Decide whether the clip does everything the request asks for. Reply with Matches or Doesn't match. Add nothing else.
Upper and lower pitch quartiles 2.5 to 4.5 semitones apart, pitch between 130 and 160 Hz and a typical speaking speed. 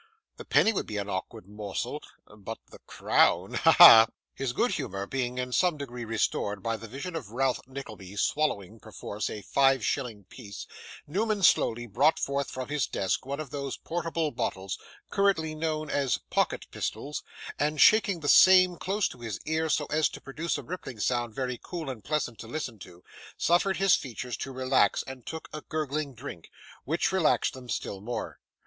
Doesn't match